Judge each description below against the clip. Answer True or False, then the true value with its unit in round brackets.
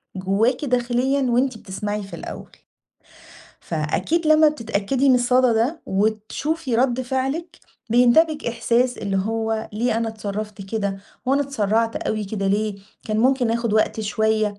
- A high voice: True (230 Hz)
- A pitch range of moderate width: True (3.5 semitones)